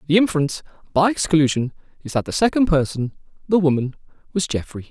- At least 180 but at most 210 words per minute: No, slow, 135 wpm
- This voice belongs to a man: Yes, male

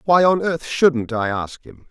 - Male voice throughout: Yes, male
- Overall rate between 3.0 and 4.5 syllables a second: Yes, 3.9 syllables/s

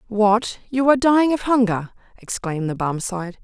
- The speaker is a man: No, female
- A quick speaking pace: No, average, 155 wpm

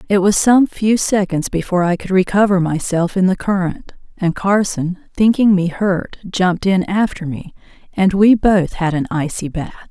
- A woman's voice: Yes, female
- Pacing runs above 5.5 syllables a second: No, 4.8 syllables/s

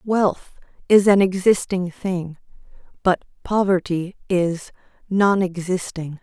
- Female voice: Yes, female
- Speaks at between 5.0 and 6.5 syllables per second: No, 3.6 syllables/s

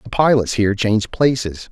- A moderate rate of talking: Yes, average, 175 wpm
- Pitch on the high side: No, low, 110 Hz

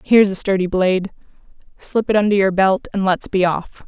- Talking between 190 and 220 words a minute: Yes, average, 200 wpm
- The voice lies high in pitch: Yes, high, 195 Hz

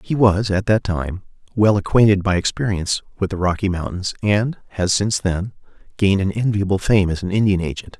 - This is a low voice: Yes, low, 100 Hz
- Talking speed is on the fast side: No, average, 190 wpm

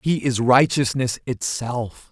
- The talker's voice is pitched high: No, low, 125 Hz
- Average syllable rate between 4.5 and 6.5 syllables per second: No, 3.6 syllables/s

